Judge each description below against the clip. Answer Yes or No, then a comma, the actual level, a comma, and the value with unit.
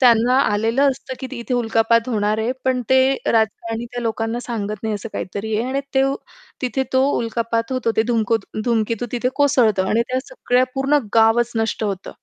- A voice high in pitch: Yes, high, 230 Hz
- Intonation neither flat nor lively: No, narrow, 2.3 semitones